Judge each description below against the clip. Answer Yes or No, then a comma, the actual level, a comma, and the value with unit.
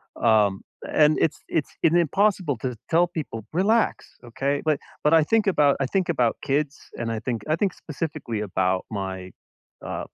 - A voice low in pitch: No, medium, 145 Hz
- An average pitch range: No, wide, 6.5 semitones